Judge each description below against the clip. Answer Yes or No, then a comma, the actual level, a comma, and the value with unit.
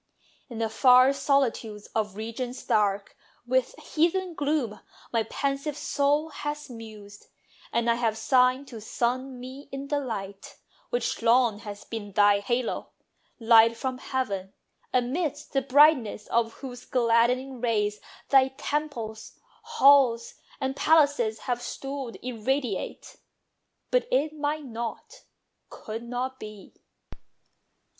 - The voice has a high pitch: Yes, very high, 250 Hz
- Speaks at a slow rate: Yes, slow, 120 wpm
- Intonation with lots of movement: No, average, 3.9 semitones